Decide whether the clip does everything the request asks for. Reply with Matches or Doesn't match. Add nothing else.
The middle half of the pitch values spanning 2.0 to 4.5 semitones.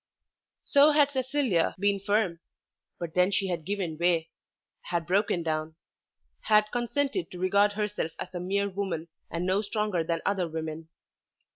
Matches